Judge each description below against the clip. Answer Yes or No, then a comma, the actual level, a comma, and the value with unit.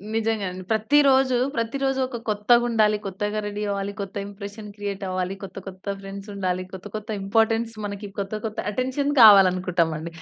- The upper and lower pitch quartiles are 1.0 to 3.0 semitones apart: Yes, narrow, 2.5 semitones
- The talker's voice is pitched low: No, high, 205 Hz